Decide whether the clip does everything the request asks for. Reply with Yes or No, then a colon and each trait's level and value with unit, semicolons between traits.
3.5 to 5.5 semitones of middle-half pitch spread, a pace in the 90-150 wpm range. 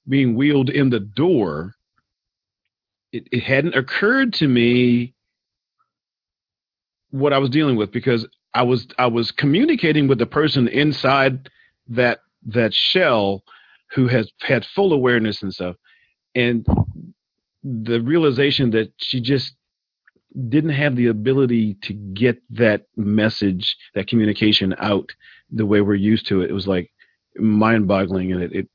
Yes: average, 4.6 semitones; average, 140 wpm